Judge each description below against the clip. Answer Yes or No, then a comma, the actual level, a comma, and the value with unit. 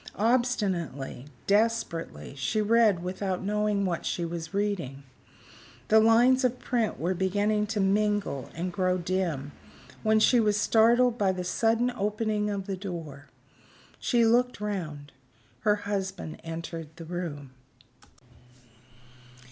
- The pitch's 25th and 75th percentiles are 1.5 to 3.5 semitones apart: No, average, 4.1 semitones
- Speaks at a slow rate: Yes, slow, 125 wpm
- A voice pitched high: Yes, high, 200 Hz